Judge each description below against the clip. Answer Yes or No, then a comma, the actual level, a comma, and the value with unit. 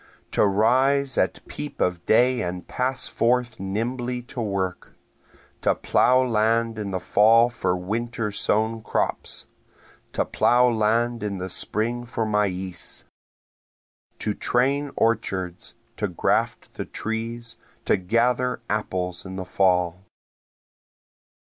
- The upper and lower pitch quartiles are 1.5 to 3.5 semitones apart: No, average, 4.1 semitones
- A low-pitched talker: Yes, low, 110 Hz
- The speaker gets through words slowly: Yes, slow, 120 wpm